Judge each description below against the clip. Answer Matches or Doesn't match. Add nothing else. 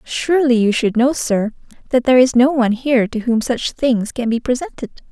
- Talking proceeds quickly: Matches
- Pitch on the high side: Matches